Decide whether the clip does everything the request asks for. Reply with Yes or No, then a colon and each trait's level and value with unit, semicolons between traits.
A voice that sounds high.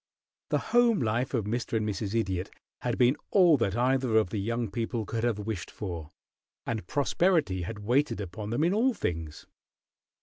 No: low, 115 Hz